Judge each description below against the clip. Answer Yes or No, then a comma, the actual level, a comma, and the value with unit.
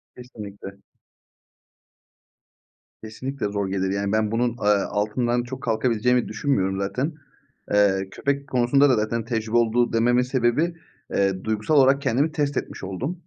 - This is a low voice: Yes, low, 120 Hz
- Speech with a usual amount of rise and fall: Yes, average, 4.0 semitones